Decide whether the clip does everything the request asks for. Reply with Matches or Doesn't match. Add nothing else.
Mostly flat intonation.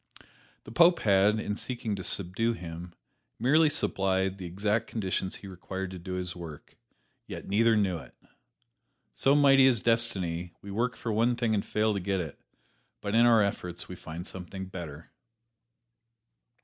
Doesn't match